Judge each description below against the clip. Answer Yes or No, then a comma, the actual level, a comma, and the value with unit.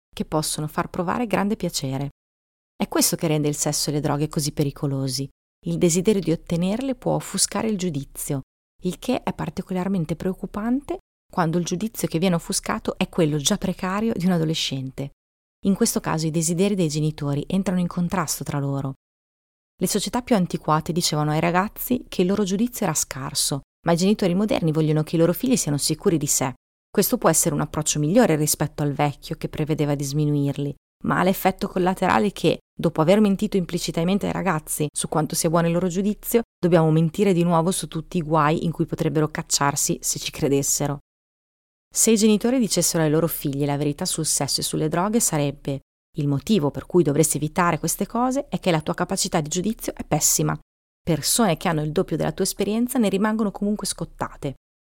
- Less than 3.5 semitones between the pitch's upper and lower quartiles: No, average, 4.4 semitones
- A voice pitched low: No, medium, 170 Hz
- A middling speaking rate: No, fast, 185 wpm